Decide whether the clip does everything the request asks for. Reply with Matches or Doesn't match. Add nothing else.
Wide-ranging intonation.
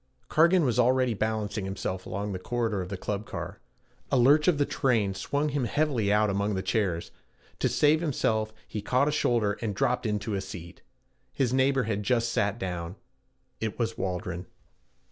Doesn't match